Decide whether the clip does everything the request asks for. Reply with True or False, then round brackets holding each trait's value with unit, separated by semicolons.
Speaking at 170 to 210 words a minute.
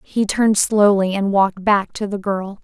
True (205 wpm)